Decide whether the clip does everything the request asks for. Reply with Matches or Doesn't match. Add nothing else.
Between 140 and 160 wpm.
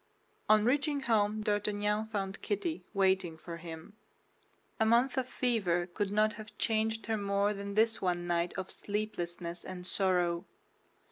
Matches